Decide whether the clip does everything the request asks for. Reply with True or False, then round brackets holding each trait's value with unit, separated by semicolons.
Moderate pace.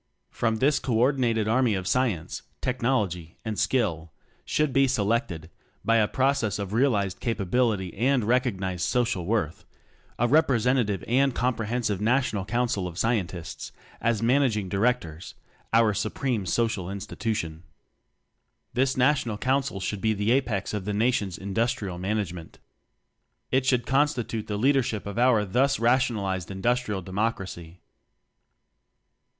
False (130 wpm)